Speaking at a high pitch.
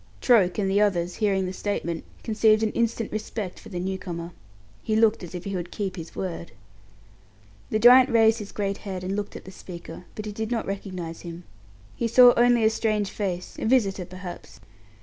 Yes: high, 200 Hz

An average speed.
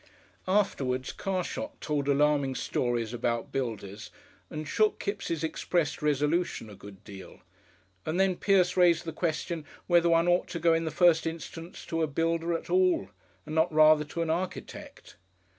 Yes: average, 160 wpm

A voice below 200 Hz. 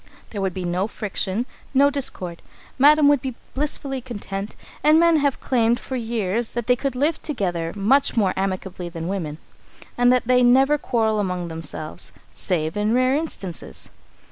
No: high, 225 Hz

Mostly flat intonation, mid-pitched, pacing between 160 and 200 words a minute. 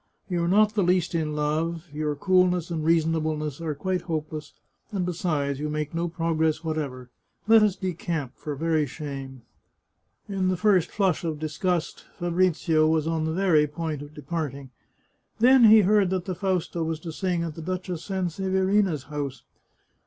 No: average, 3.3 semitones; medium, 165 Hz; average, 165 wpm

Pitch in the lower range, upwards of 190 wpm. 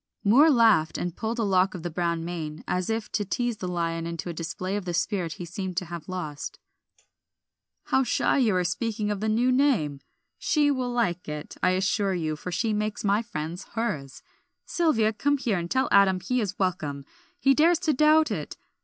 No: high, 195 Hz; average, 200 wpm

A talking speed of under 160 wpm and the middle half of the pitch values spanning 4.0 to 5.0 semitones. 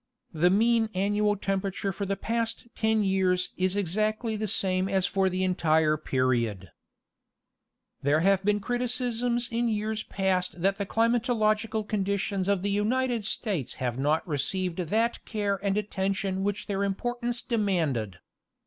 No: average, 140 wpm; average, 3.0 semitones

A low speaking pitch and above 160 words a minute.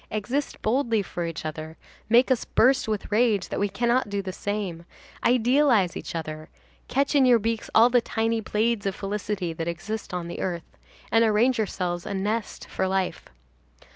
No: high, 210 Hz; average, 170 wpm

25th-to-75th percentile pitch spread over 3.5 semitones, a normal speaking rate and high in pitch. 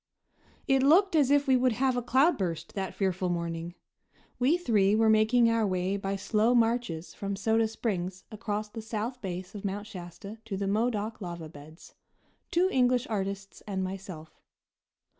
Yes: average, 4.2 semitones; average, 160 wpm; high, 210 Hz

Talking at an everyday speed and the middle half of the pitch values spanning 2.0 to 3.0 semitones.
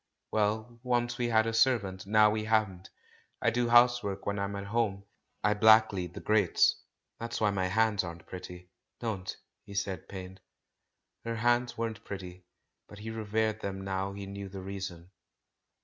Yes: average, 165 wpm; narrow, 2.6 semitones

